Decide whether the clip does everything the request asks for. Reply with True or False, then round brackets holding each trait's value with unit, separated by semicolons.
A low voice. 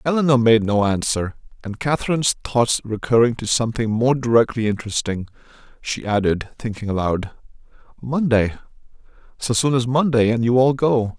True (120 Hz)